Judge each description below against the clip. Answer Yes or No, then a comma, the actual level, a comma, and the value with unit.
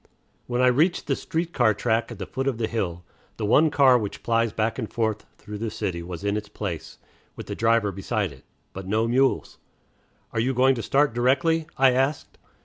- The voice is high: No, low, 115 Hz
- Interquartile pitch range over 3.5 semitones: Yes, average, 4.0 semitones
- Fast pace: Yes, fast, 210 wpm